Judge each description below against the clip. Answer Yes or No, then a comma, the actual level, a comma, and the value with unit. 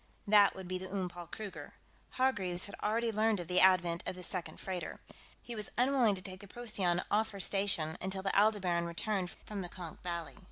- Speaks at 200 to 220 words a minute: Yes, fast, 205 wpm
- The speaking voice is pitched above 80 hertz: Yes, high, 190 Hz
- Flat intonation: No, average, 3.0 semitones